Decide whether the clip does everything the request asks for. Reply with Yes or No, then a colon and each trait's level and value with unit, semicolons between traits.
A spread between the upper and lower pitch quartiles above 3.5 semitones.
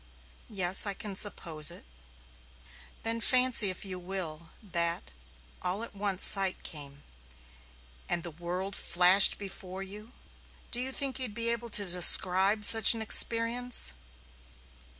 Yes: average, 4.1 semitones